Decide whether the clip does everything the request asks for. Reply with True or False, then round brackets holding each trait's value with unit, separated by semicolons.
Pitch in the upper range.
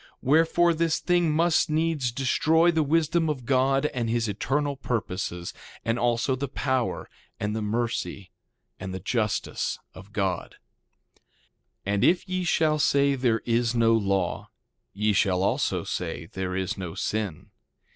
False (120 Hz)